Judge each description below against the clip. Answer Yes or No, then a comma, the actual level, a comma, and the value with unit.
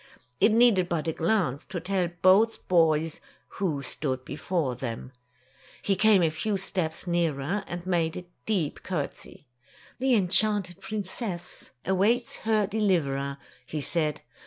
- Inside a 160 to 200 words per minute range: No, slow, 135 wpm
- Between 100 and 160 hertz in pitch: No, medium, 175 Hz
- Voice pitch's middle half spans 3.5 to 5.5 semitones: Yes, average, 4.3 semitones